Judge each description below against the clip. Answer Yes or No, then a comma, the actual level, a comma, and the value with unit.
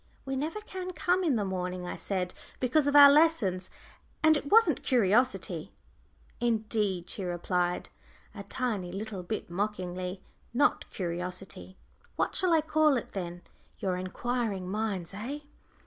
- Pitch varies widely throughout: Yes, wide, 7.6 semitones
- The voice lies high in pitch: Yes, high, 210 Hz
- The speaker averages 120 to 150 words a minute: Yes, average, 140 wpm